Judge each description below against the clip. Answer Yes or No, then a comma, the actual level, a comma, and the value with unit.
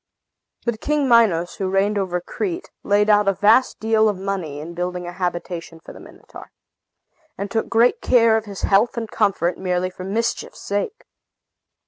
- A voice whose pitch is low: No, high, 200 Hz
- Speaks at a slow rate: No, average, 170 wpm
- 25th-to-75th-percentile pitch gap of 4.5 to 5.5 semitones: No, average, 3.8 semitones